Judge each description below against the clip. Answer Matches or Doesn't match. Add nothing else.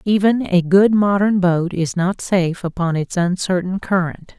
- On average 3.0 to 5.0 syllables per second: Matches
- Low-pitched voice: Doesn't match